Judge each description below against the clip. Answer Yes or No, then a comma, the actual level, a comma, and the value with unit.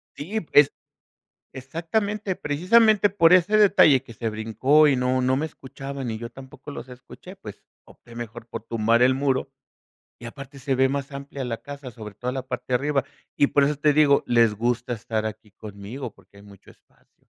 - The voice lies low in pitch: Yes, low, 130 Hz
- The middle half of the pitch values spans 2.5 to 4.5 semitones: Yes, average, 3.8 semitones